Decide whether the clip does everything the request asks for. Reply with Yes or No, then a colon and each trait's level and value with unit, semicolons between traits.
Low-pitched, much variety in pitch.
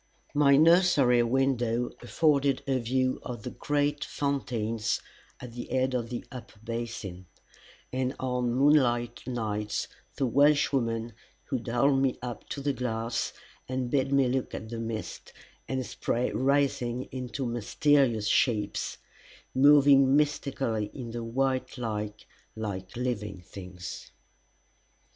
No: low, 125 Hz; average, 3.0 semitones